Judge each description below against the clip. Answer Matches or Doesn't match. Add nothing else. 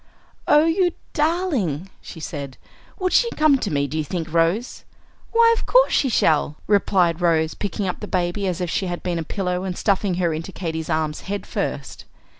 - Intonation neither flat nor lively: Doesn't match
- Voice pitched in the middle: Matches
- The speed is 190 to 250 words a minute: Matches